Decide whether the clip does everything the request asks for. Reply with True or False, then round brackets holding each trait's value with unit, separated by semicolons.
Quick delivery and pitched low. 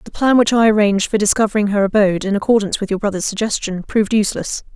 False (215 wpm; 205 Hz)